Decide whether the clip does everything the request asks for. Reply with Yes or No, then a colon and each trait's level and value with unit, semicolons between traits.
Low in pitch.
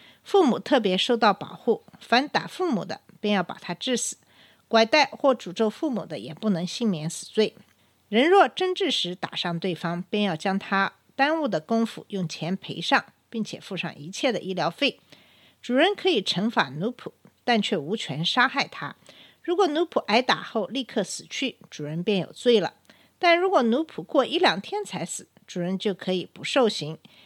No: high, 215 Hz